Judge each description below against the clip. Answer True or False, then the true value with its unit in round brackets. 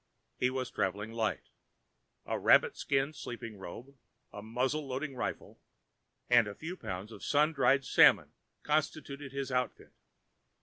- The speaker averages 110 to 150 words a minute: True (135 wpm)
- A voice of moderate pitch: False (130 Hz)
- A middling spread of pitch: True (3.7 semitones)